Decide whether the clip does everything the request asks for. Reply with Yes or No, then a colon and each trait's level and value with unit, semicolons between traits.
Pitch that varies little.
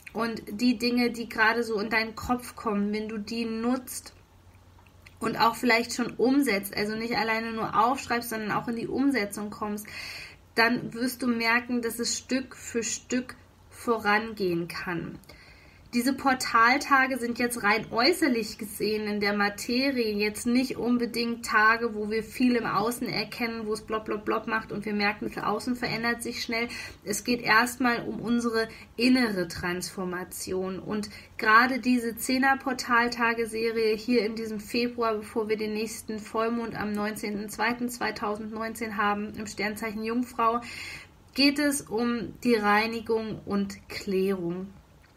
Yes: narrow, 2.2 semitones